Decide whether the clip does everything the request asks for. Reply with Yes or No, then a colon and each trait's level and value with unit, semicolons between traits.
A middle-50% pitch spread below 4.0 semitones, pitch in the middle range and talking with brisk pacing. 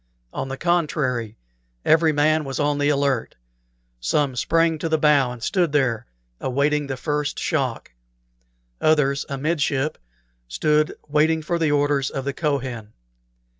No: narrow, 2.6 semitones; medium, 145 Hz; slow, 135 wpm